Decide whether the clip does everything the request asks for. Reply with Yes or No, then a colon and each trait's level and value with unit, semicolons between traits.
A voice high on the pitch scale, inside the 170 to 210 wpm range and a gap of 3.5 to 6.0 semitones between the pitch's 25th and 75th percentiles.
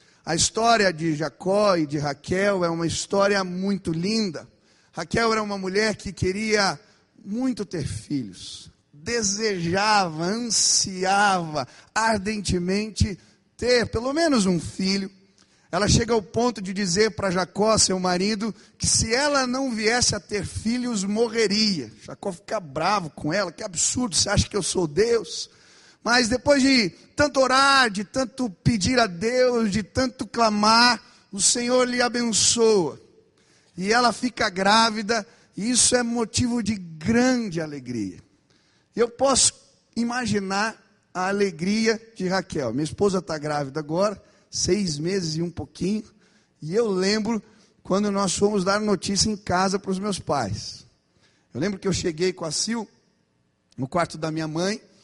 No: high, 205 Hz; average, 145 wpm; average, 4.2 semitones